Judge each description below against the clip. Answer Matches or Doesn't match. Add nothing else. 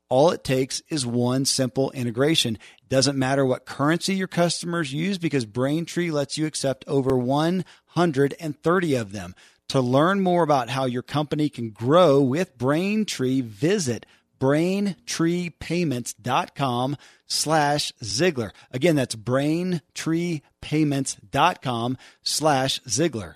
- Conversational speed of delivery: Doesn't match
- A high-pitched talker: Doesn't match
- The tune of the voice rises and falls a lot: Doesn't match